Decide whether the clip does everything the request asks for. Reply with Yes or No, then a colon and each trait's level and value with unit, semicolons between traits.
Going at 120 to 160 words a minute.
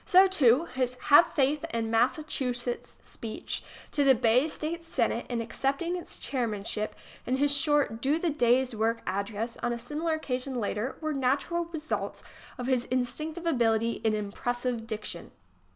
Yes: average, 155 wpm